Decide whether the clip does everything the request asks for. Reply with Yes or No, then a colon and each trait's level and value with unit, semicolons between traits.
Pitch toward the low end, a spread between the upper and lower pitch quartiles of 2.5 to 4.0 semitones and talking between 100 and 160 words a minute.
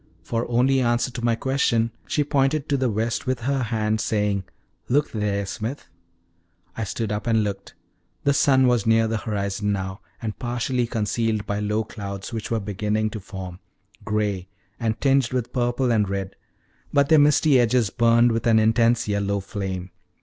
No: low, 115 Hz; average, 3.0 semitones; average, 170 wpm